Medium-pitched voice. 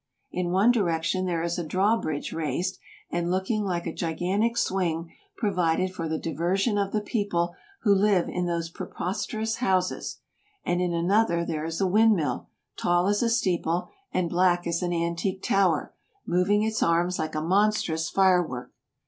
Yes: medium, 180 Hz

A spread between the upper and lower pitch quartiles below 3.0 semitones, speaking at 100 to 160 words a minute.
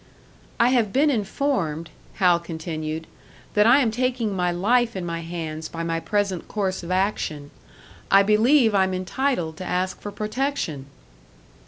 No: wide, 5.5 semitones; average, 150 wpm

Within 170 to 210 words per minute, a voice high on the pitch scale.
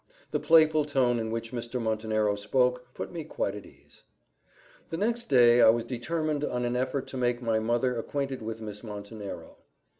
No: average, 185 wpm; low, 120 Hz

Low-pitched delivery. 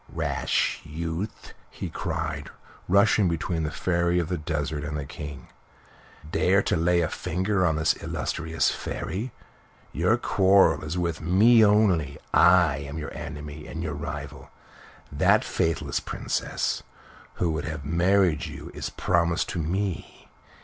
Yes: very low, 85 Hz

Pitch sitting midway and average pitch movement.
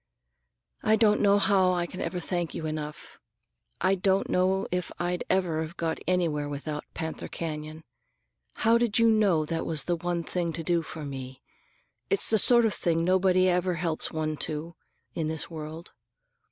Yes: medium, 175 Hz; average, 3.0 semitones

